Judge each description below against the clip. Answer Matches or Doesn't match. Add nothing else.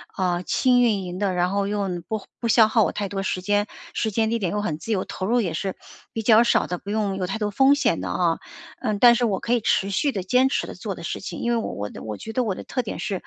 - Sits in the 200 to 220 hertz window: Matches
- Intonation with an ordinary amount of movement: Matches